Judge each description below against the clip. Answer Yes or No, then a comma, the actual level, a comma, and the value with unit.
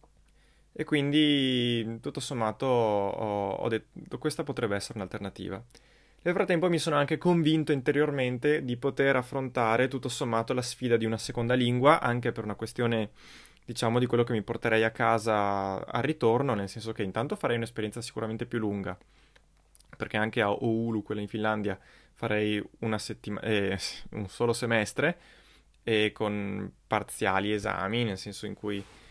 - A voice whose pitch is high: No, low, 115 Hz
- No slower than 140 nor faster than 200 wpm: Yes, average, 155 wpm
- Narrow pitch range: No, average, 3.3 semitones